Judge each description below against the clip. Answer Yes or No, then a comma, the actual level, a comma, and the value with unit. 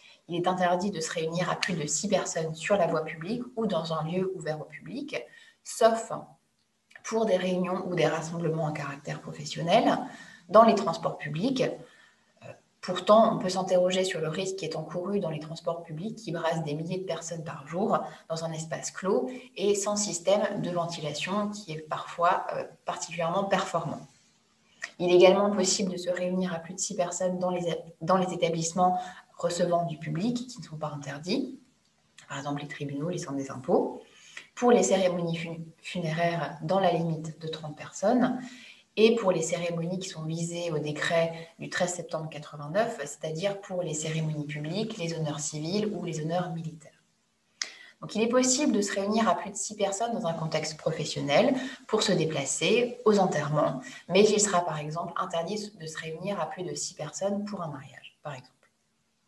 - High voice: No, medium, 175 Hz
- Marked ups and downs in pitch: No, average, 3.9 semitones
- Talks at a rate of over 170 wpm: Yes, average, 180 wpm